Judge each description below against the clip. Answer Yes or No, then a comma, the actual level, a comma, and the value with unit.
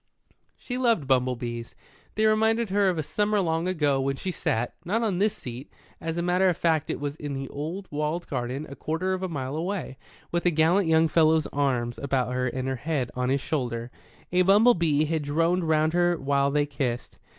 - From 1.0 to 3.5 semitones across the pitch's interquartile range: No, average, 4.9 semitones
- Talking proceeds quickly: Yes, fast, 210 wpm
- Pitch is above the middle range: No, medium, 155 Hz